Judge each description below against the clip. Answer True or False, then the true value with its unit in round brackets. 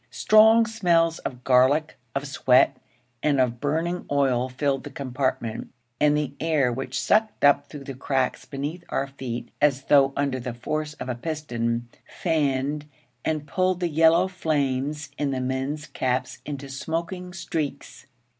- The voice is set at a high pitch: False (145 Hz)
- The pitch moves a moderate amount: True (3.5 semitones)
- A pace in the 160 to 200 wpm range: False (150 wpm)